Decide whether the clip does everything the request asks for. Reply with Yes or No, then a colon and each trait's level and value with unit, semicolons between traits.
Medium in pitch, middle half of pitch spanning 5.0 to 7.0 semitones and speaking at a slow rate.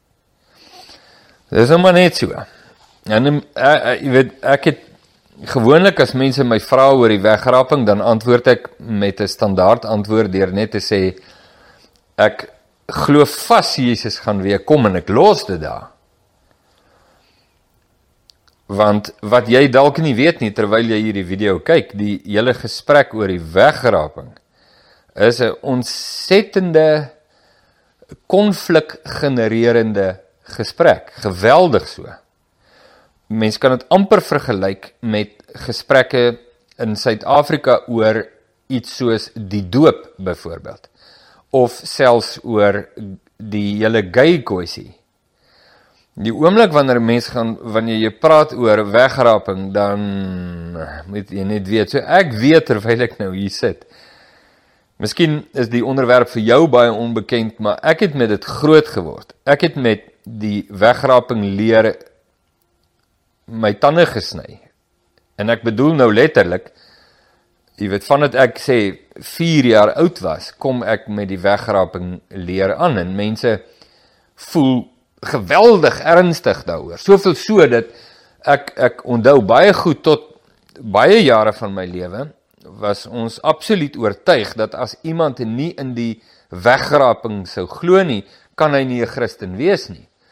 No: low, 115 Hz; average, 5.3 semitones; slow, 130 wpm